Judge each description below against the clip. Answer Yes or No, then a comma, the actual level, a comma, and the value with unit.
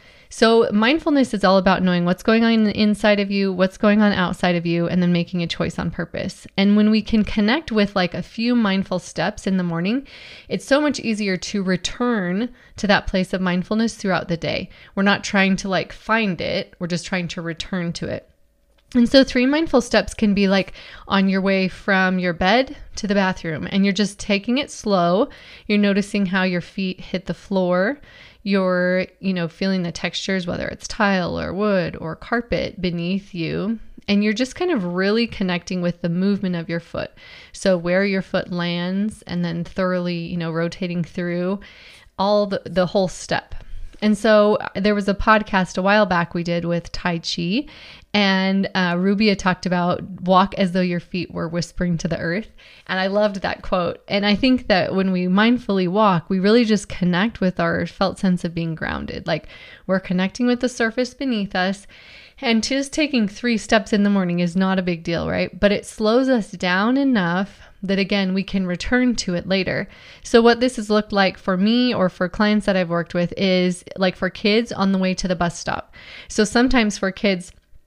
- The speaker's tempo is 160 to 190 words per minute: No, average, 200 wpm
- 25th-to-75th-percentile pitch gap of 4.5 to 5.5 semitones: No, average, 2.9 semitones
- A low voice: No, high, 195 Hz